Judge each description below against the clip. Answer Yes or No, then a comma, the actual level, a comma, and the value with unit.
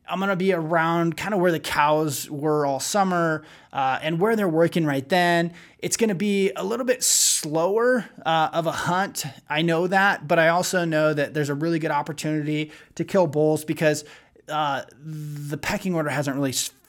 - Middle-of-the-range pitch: Yes, medium, 160 Hz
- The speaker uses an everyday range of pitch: Yes, average, 3.0 semitones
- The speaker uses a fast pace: No, average, 190 wpm